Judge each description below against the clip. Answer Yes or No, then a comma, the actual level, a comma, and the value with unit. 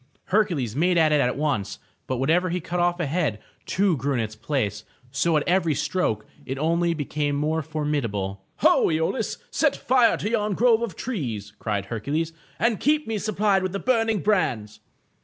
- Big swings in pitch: Yes, wide, 6.4 semitones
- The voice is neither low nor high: Yes, medium, 160 Hz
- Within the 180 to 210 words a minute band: Yes, average, 190 wpm